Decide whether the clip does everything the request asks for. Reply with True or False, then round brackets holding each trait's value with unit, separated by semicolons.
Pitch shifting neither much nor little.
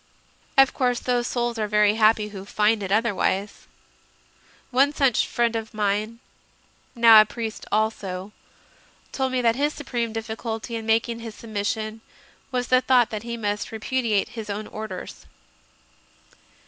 False (2.1 semitones)